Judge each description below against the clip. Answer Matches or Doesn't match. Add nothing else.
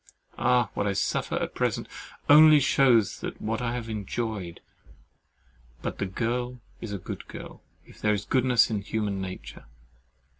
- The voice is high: Doesn't match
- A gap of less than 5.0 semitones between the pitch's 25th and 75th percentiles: Matches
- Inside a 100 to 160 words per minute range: Matches